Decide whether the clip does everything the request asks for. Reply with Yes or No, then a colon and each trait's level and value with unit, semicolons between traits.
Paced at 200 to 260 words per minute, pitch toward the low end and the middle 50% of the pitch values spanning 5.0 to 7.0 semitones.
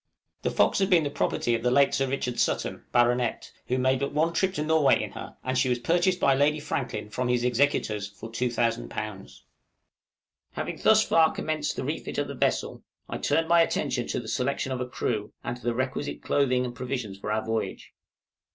No: fast, 205 wpm; low, 125 Hz; average, 3.3 semitones